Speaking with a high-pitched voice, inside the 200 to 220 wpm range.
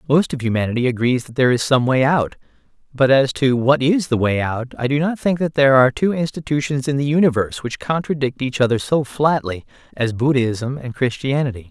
No: low, 135 Hz; fast, 205 wpm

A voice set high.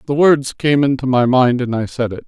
No: low, 130 Hz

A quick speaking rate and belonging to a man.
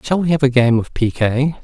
Yes: fast, 255 wpm; male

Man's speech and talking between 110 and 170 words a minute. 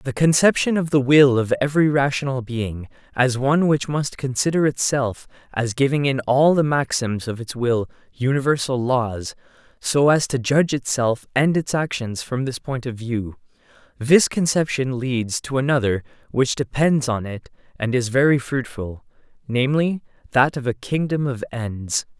Yes: male; average, 160 wpm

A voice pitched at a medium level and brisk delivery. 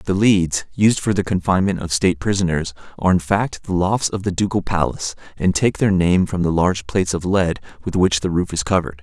No: very low, 90 Hz; fast, 225 wpm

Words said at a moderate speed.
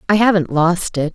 No: fast, 210 wpm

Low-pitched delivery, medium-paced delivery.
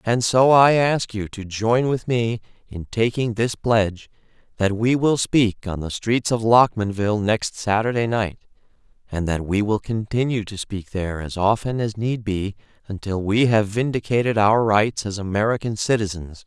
Yes: low, 110 Hz; average, 170 wpm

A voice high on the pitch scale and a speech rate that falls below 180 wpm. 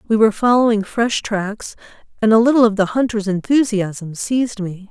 Yes: high, 215 Hz; average, 170 wpm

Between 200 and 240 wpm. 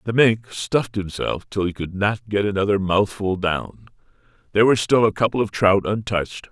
No: average, 185 wpm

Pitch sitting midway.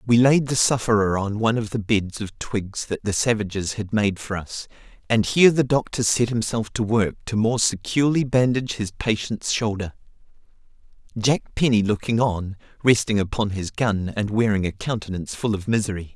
No: low, 110 Hz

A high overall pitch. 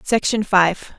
Yes: high, 200 Hz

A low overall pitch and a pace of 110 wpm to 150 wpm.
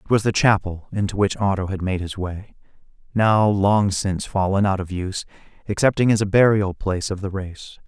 No: low, 100 Hz; average, 200 wpm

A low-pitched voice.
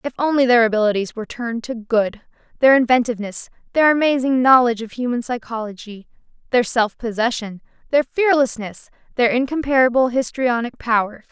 No: high, 240 Hz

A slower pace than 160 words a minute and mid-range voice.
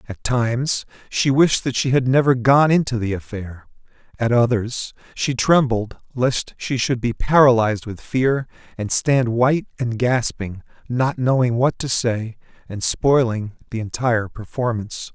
No: average, 150 wpm; low, 120 Hz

